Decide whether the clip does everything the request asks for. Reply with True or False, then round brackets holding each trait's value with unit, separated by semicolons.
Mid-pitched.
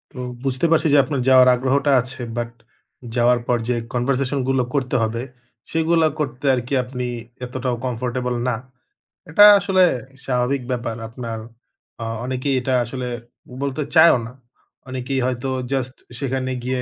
False (130 Hz)